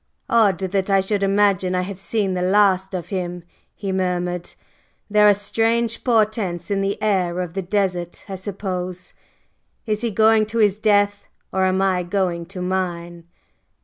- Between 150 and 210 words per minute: Yes, average, 165 wpm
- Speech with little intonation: Yes, narrow, 2.3 semitones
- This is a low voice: No, high, 195 Hz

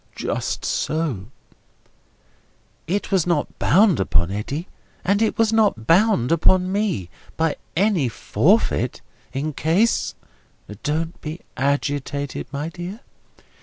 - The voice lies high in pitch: No, medium, 165 Hz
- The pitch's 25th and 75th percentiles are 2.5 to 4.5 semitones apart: No, wide, 5.5 semitones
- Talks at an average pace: No, slow, 110 wpm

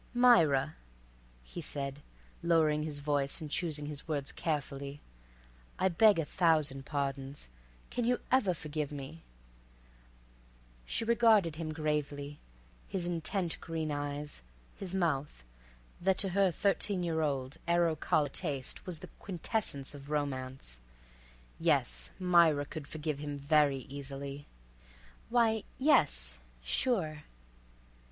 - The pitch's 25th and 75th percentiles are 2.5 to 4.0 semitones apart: Yes, average, 3.6 semitones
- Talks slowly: Yes, slow, 115 wpm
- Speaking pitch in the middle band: Yes, medium, 150 Hz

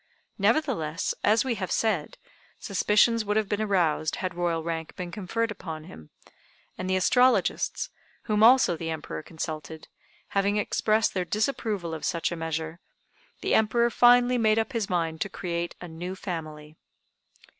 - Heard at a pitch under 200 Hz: Yes, medium, 185 Hz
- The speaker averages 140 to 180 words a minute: Yes, average, 155 wpm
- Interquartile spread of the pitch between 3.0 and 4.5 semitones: No, average, 5.0 semitones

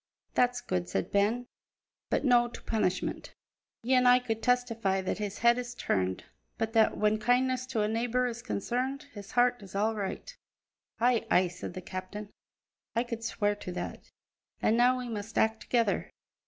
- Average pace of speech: Yes, average, 175 wpm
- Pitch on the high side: Yes, high, 230 Hz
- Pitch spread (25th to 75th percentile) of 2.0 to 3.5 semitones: Yes, average, 3.2 semitones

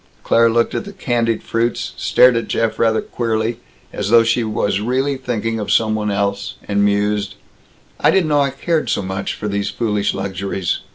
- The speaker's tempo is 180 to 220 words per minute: Yes, average, 185 wpm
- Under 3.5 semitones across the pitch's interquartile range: Yes, average, 2.9 semitones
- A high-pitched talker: No, low, 110 Hz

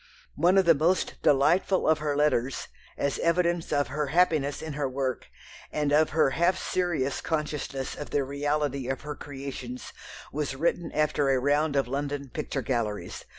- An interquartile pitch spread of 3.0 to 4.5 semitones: No, narrow, 2.5 semitones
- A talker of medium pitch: Yes, medium, 145 Hz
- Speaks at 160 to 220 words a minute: Yes, average, 165 wpm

